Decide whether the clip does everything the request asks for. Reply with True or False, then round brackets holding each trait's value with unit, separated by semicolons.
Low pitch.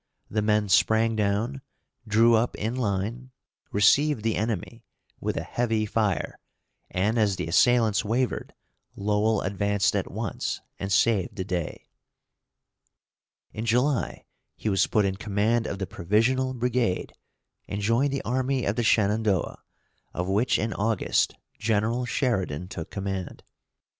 True (110 Hz)